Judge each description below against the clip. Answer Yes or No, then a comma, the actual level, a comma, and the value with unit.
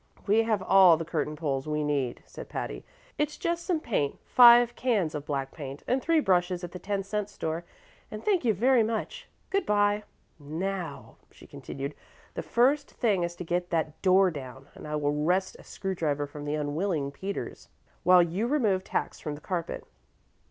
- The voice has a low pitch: No, medium, 180 Hz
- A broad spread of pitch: Yes, wide, 6.1 semitones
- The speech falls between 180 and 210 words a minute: Yes, average, 185 wpm